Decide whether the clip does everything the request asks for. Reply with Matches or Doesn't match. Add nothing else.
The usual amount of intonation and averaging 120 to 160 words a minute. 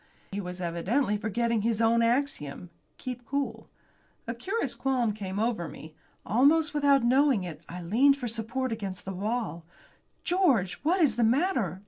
Doesn't match